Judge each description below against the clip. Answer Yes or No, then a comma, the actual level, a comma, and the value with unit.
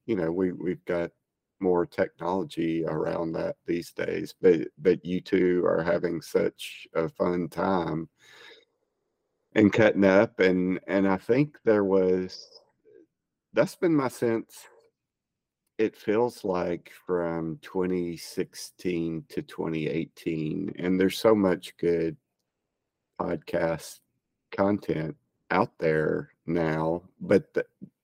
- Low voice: Yes, very low, 90 Hz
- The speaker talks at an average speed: No, slow, 115 wpm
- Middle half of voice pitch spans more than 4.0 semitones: Yes, average, 4.5 semitones